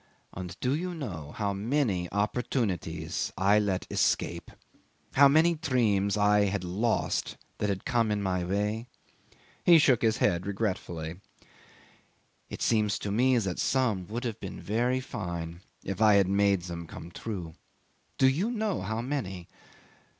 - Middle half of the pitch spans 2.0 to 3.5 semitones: No, average, 5.0 semitones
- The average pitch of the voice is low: Yes, low, 105 Hz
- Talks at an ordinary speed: Yes, average, 150 wpm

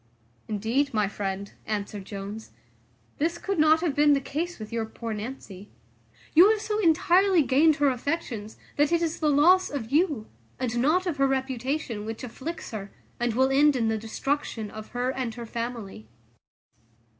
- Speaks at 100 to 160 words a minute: No, average, 170 wpm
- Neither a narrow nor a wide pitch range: No, wide, 5.8 semitones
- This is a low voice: No, very high, 260 Hz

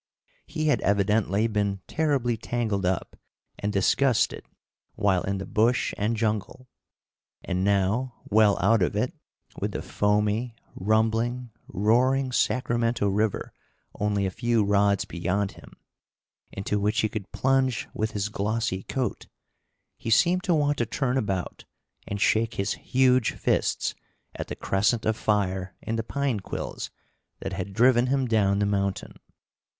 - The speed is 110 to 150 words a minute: Yes, average, 145 wpm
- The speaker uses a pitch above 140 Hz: No, low, 110 Hz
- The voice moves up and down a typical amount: Yes, average, 3.4 semitones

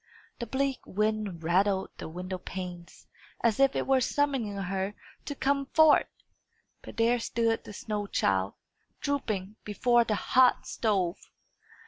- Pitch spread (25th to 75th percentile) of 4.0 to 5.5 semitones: Yes, average, 5.1 semitones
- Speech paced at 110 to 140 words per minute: Yes, slow, 135 wpm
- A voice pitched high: Yes, high, 215 Hz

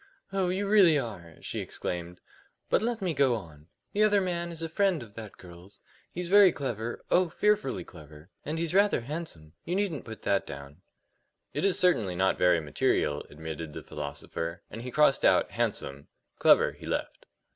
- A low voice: Yes, low, 120 Hz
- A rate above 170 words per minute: Yes, average, 180 wpm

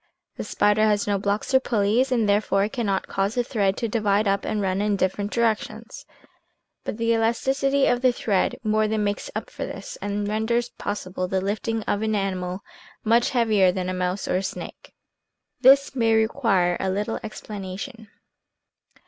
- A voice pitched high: Yes, high, 210 Hz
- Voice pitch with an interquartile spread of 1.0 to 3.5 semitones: Yes, average, 2.7 semitones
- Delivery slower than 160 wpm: No, average, 175 wpm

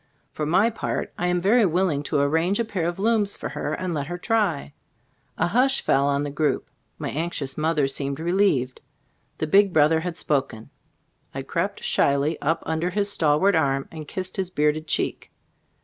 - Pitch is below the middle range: No, medium, 160 Hz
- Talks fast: No, average, 180 wpm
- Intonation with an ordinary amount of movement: Yes, average, 4.4 semitones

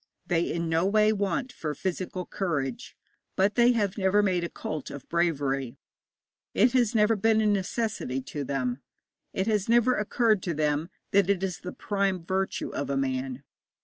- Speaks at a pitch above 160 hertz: Yes, medium, 185 Hz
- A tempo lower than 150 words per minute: No, average, 175 wpm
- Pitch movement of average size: No, wide, 5.8 semitones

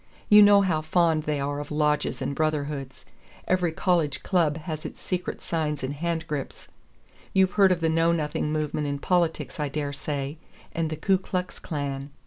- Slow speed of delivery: No, average, 175 wpm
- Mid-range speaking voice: Yes, medium, 155 Hz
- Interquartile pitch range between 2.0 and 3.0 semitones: Yes, average, 2.7 semitones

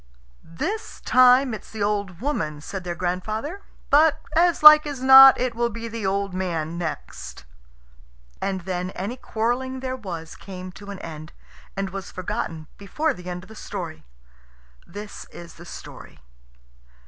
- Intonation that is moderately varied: No, wide, 6.2 semitones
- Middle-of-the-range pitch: No, high, 200 Hz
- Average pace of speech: Yes, average, 155 wpm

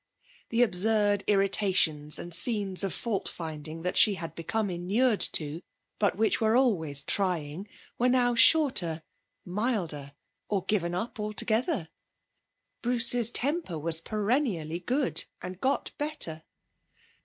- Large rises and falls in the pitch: Yes, wide, 5.8 semitones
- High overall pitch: Yes, high, 200 Hz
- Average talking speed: No, slow, 120 wpm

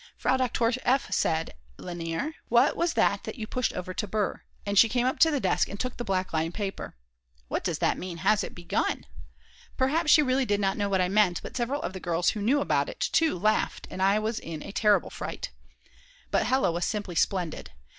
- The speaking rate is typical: No, fast, 215 wpm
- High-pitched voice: Yes, high, 210 Hz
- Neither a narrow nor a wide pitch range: No, wide, 5.7 semitones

